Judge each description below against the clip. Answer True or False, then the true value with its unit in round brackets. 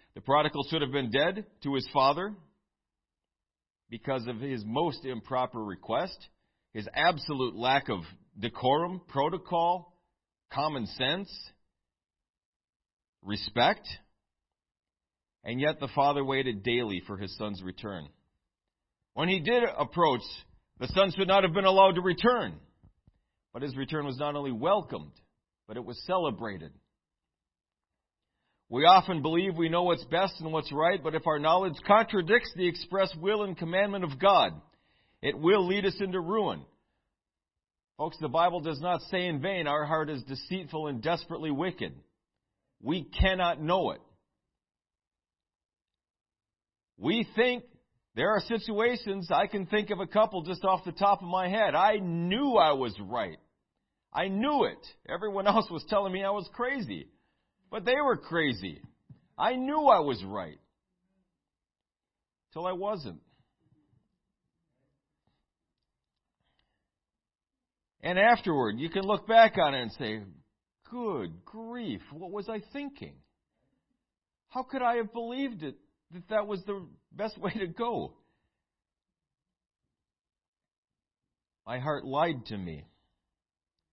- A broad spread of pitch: True (8.3 semitones)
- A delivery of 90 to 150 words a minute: True (135 wpm)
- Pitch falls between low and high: True (170 Hz)